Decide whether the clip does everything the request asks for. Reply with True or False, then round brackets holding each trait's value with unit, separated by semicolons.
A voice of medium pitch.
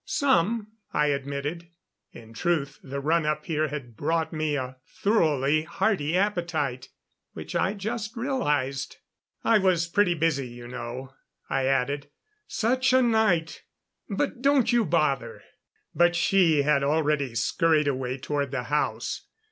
True (155 Hz)